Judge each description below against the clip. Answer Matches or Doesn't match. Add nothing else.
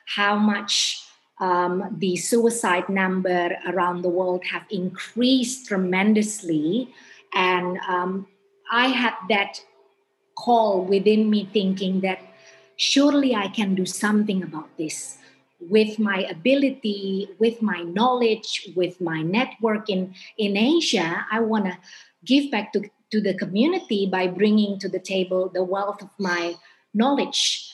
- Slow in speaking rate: Matches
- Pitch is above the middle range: Matches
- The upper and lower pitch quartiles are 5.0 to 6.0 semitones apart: Doesn't match